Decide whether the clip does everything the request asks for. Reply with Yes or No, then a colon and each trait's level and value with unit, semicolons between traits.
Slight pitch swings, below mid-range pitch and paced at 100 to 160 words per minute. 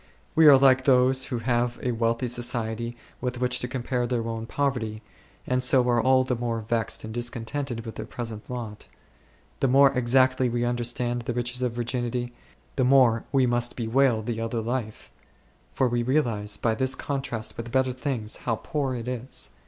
No: narrow, 1.9 semitones; low, 120 Hz; average, 180 wpm